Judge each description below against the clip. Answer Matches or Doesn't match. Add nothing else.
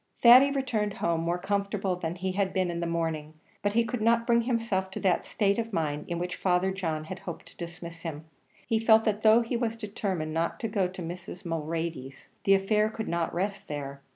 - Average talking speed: Doesn't match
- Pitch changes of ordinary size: Matches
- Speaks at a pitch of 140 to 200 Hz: Matches